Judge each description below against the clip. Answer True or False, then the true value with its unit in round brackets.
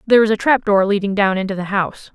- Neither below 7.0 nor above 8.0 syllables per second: True (7.1 syllables/s)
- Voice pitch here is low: False (205 Hz)